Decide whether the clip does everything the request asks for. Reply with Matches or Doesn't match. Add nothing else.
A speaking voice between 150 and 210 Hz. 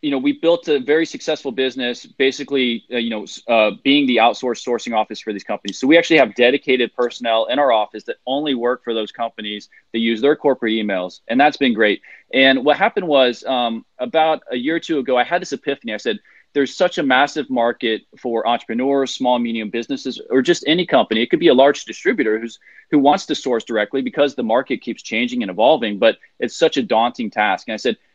Doesn't match